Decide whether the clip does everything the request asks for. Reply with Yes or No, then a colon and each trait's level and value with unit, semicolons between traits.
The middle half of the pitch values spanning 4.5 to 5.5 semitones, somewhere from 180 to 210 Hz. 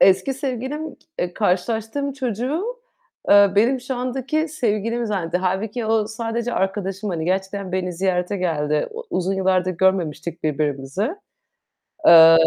Yes: average, 5.2 semitones; high, 200 Hz